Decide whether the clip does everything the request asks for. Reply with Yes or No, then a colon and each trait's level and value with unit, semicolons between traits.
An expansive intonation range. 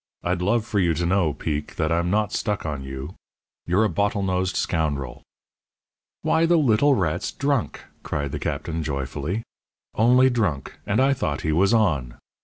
Yes: wide, 6.1 semitones